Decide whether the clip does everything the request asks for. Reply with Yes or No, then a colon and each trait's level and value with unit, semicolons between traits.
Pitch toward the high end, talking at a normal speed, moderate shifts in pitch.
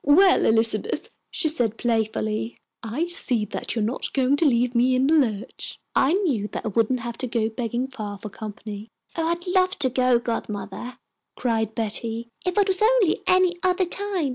No: high, 245 Hz; average, 190 wpm; wide, 6.9 semitones